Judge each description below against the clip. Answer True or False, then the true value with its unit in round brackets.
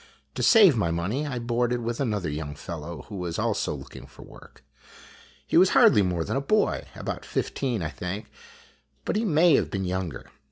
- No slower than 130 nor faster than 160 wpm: False (190 wpm)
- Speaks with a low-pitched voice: True (105 Hz)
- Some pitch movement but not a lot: False (7.6 semitones)